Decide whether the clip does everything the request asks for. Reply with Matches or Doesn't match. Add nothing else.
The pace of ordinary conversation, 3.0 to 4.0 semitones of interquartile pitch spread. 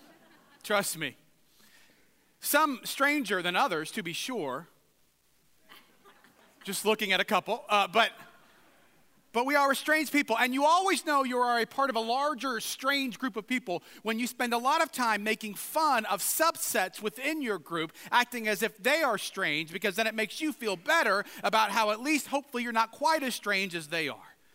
Doesn't match